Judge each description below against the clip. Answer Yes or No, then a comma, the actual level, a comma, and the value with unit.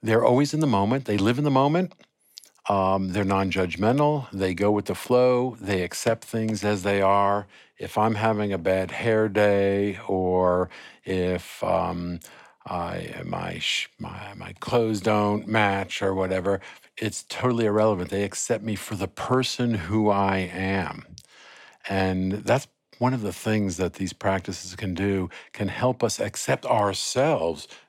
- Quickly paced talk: No, average, 155 wpm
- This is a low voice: Yes, low, 100 Hz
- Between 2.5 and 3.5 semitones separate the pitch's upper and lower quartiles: Yes, average, 2.9 semitones